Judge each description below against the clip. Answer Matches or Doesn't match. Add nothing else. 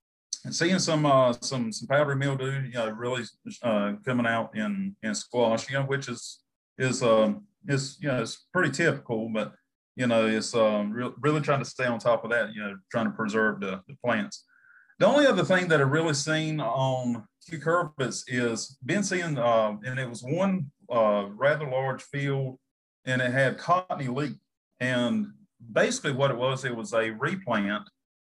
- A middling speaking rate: Matches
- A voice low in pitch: Matches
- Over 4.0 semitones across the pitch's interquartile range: Matches